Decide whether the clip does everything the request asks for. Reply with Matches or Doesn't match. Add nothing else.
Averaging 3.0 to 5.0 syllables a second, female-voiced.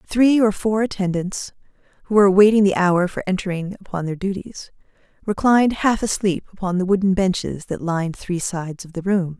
Doesn't match